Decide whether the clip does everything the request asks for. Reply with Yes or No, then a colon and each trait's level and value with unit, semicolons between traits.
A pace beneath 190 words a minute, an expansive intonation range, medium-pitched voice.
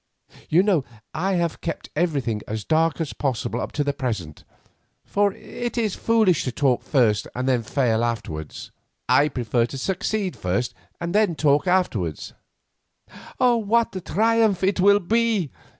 Yes: average, 145 wpm; wide, 8.4 semitones; medium, 160 Hz